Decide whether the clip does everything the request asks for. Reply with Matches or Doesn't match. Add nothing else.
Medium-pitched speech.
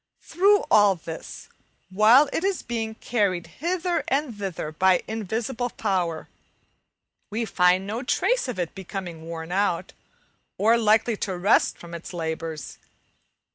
Doesn't match